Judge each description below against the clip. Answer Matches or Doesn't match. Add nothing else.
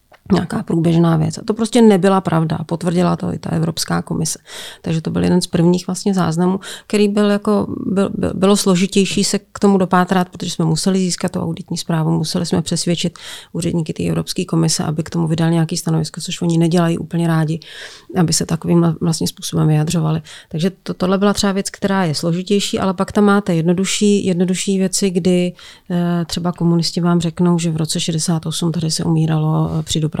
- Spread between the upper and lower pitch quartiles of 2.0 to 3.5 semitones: Matches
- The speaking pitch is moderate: Matches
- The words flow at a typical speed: Doesn't match